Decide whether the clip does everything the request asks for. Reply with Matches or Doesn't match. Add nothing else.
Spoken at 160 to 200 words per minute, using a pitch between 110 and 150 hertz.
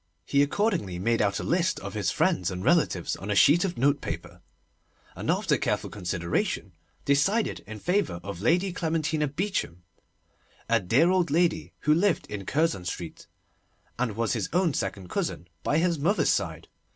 Matches